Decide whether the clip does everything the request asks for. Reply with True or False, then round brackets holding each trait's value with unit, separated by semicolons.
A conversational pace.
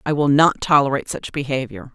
True (185 wpm)